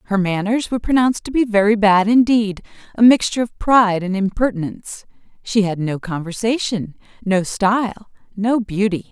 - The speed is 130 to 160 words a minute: Yes, average, 150 wpm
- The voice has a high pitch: Yes, high, 210 Hz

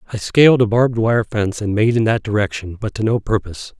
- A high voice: No, low, 110 Hz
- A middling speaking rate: No, fast, 235 wpm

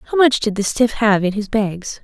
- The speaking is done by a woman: Yes, female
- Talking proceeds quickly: Yes, fast, 265 wpm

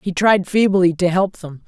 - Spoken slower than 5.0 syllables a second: Yes, 4.5 syllables/s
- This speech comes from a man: No, female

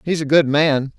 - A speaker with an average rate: No, fast, 245 wpm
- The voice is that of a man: Yes, male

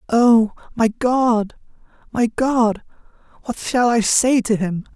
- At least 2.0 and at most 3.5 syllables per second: Yes, 3.3 syllables/s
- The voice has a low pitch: No, high, 230 Hz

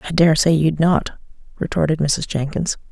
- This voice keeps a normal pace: Yes, average, 165 wpm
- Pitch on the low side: No, medium, 155 Hz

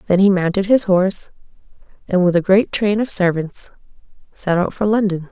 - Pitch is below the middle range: No, high, 190 Hz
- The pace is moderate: Yes, average, 180 wpm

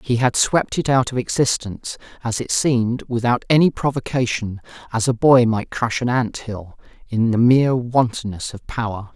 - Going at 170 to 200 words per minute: Yes, average, 175 wpm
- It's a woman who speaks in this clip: No, male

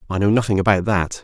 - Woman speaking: No, male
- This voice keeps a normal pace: No, fast, 245 wpm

